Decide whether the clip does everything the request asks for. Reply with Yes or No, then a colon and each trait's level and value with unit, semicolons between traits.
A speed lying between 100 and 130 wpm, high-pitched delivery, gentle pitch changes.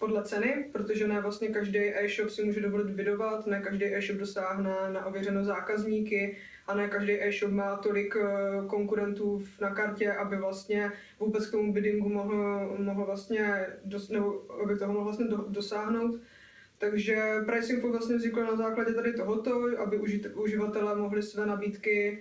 No: average, 150 wpm; high, 205 Hz; narrow, 1.0 semitones